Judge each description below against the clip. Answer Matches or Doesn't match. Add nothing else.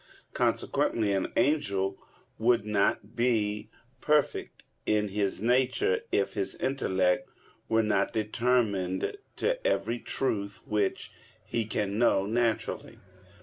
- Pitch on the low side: Matches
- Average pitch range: Matches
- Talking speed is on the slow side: Matches